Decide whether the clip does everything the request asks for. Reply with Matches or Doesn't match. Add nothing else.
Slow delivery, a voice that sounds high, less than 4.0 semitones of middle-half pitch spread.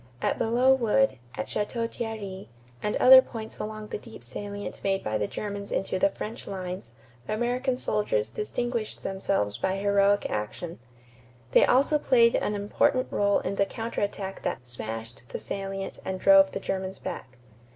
Doesn't match